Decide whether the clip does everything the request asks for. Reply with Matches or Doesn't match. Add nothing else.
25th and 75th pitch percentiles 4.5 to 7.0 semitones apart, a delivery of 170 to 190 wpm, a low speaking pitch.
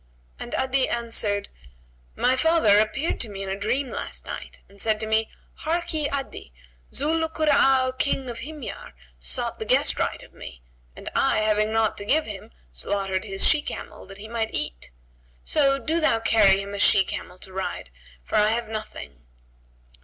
Doesn't match